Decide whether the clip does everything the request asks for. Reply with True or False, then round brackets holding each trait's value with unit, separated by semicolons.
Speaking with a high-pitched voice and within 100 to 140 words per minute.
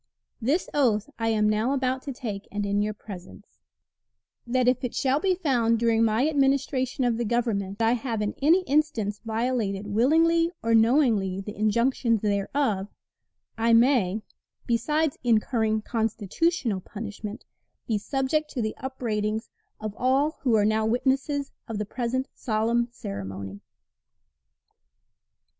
True (230 Hz; 135 wpm)